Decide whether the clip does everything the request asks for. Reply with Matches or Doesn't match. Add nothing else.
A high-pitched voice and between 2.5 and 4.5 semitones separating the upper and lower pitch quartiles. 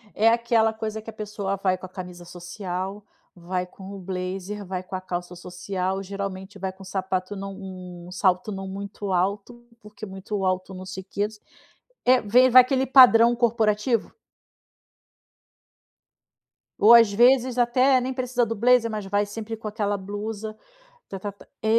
Matches